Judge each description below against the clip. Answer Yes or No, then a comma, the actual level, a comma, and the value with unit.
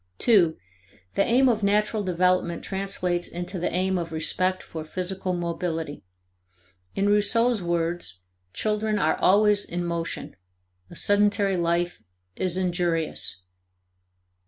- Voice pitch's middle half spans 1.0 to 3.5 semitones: Yes, average, 2.9 semitones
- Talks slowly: Yes, slow, 115 wpm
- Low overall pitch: No, medium, 185 Hz